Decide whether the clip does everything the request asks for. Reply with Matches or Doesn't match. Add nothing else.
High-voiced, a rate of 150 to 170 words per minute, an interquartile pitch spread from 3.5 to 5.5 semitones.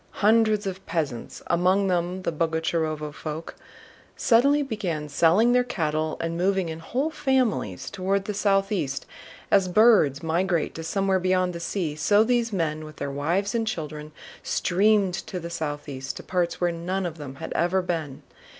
Doesn't match